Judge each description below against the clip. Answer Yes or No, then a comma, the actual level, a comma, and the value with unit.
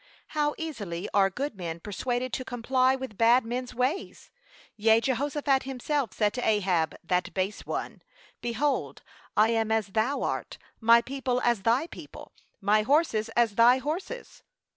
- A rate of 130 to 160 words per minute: Yes, average, 150 wpm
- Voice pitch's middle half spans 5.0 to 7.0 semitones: No, average, 3.8 semitones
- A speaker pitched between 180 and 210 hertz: No, high, 235 Hz